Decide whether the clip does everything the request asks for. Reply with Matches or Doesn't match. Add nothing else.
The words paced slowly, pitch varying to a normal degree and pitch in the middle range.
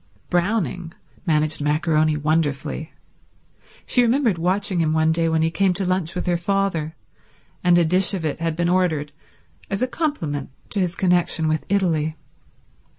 Doesn't match